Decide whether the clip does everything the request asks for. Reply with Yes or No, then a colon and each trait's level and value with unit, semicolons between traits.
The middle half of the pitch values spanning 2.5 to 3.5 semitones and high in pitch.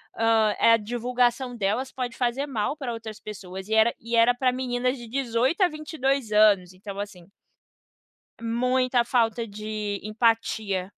Yes: average, 2.9 semitones; high, 230 Hz